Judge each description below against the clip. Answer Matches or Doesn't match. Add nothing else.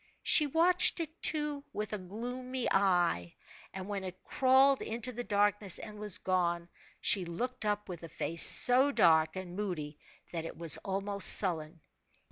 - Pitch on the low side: Doesn't match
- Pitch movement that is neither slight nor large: Doesn't match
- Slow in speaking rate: Doesn't match